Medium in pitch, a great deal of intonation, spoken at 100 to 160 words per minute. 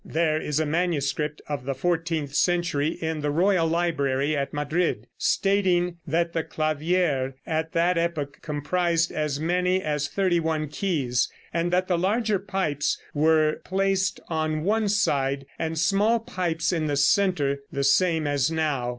No: medium, 160 Hz; average, 3.4 semitones; average, 150 wpm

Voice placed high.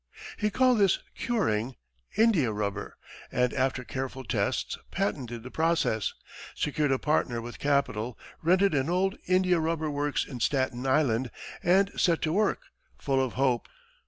No: medium, 140 Hz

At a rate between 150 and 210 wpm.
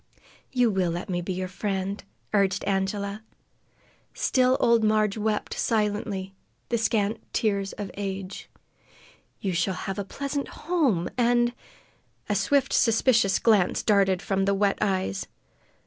No: slow, 135 wpm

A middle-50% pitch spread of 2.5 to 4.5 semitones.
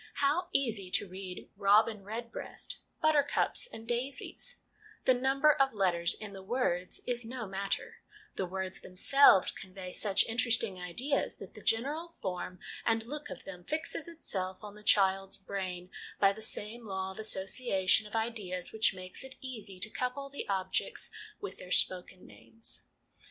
No: average, 5.0 semitones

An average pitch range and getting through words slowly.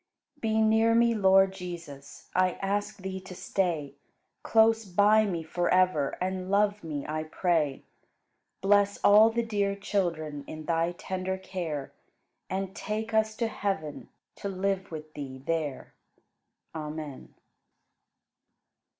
Yes: average, 4.3 semitones; slow, 125 wpm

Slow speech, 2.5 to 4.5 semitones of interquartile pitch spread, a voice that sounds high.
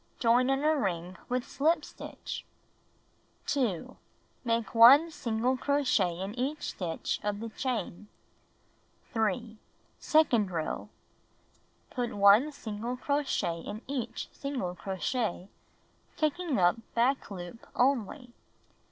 No: slow, 110 wpm; average, 5.1 semitones; high, 235 Hz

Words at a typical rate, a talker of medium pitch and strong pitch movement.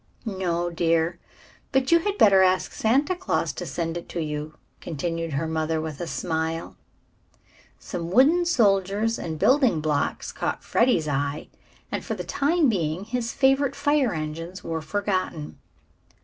Yes: average, 150 wpm; medium, 175 Hz; wide, 7.4 semitones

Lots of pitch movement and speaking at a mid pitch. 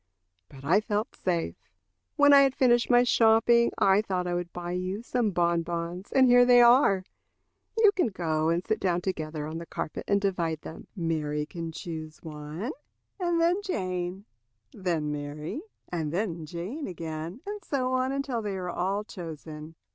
Yes: wide, 6.5 semitones; medium, 180 Hz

